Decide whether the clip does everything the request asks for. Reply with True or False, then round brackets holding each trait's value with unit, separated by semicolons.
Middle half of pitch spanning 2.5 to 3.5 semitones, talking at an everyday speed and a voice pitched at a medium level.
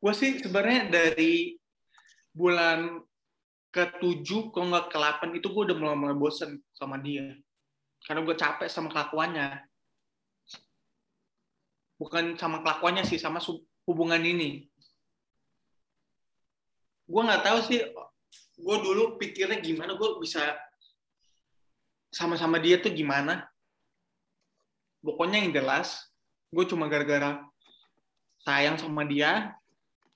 False (4.9 semitones; 100 wpm; 170 Hz)